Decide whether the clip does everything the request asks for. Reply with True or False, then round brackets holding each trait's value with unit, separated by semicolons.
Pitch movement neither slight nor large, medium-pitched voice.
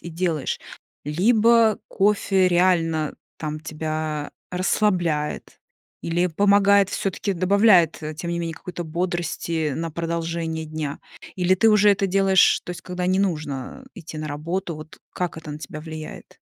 True (3.2 semitones; 170 Hz)